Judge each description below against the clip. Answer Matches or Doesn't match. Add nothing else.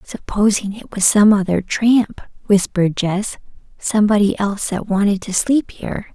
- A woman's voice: Matches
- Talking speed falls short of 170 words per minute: Matches